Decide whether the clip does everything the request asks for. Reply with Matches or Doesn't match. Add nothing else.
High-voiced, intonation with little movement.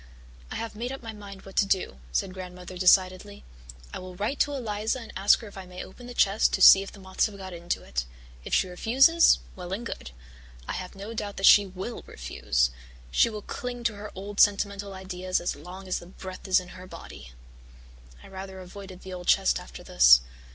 Matches